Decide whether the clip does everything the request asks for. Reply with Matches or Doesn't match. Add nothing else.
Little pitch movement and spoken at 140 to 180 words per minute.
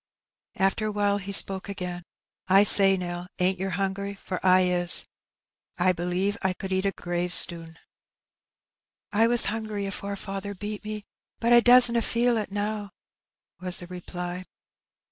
Matches